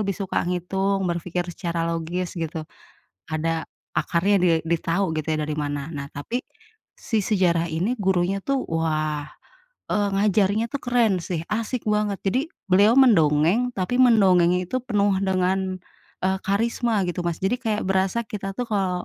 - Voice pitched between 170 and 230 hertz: Yes, high, 190 Hz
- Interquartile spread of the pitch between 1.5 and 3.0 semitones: No, average, 3.8 semitones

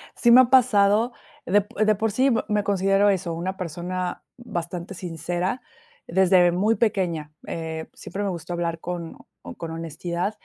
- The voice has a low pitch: No, medium, 185 Hz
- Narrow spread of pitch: No, average, 3.3 semitones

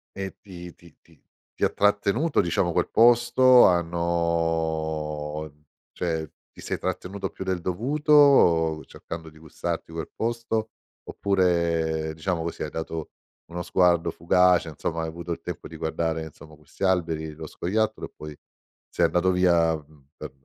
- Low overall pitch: Yes, very low, 85 Hz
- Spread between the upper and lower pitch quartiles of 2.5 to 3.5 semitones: Yes, average, 2.8 semitones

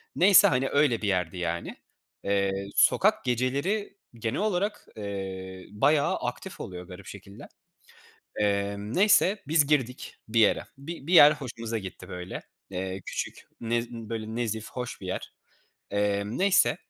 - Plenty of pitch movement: Yes, wide, 6.3 semitones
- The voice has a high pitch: No, low, 115 Hz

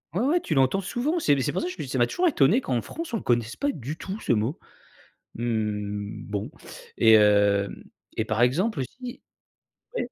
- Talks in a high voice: No, low, 130 Hz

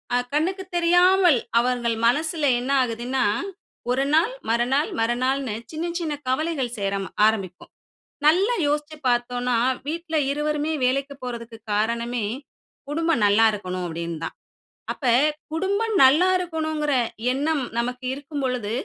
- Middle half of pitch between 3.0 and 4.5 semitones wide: No, average, 5.1 semitones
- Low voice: No, very high, 265 Hz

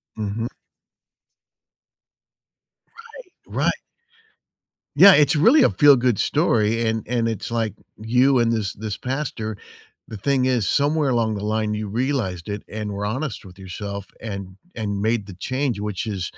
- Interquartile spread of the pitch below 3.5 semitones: No, average, 3.8 semitones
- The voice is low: Yes, low, 110 Hz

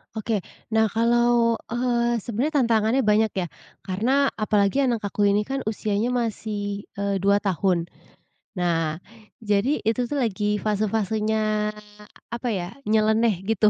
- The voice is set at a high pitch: Yes, high, 215 Hz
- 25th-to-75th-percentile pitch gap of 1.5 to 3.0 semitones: Yes, narrow, 2.6 semitones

